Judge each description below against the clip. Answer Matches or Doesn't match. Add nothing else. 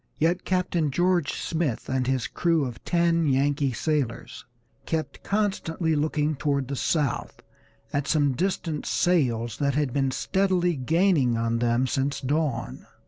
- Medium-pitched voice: Matches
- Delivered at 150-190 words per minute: Doesn't match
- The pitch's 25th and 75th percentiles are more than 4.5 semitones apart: Doesn't match